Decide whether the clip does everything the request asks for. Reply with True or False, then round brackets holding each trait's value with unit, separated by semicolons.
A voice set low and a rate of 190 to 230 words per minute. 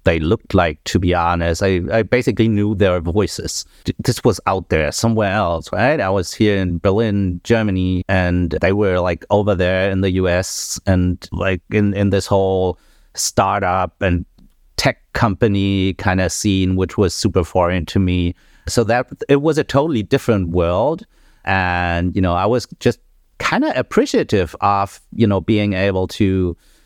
False (95 Hz; 170 wpm)